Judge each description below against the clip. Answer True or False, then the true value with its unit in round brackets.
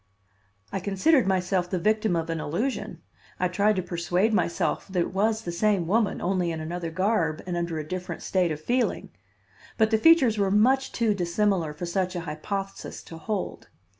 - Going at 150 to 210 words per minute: True (185 wpm)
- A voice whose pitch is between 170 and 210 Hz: True (185 Hz)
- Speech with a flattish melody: False (3.8 semitones)